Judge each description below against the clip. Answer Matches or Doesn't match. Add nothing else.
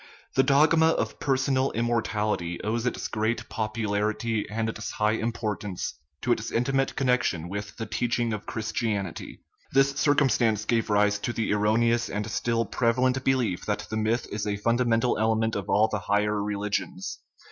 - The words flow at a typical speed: Matches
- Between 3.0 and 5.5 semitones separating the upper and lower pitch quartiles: Doesn't match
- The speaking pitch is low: Matches